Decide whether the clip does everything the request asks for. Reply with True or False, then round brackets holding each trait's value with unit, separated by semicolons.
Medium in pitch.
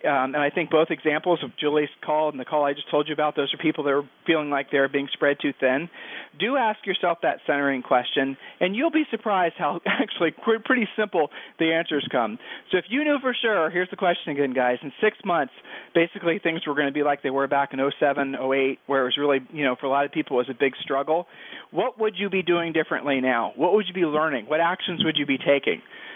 True (150 Hz)